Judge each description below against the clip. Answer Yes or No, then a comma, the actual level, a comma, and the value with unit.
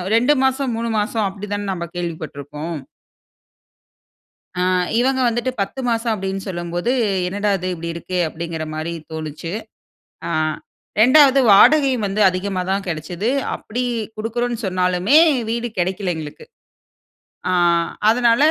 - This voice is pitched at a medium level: No, high, 195 Hz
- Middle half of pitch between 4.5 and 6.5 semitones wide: Yes, wide, 5.4 semitones